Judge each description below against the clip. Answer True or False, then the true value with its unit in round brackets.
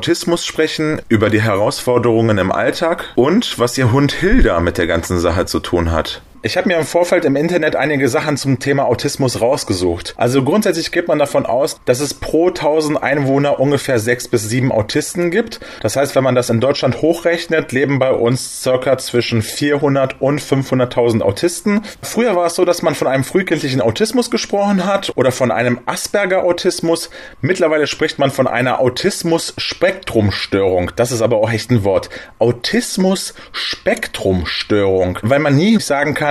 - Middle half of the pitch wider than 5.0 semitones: True (5.5 semitones)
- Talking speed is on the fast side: False (170 wpm)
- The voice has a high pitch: False (140 Hz)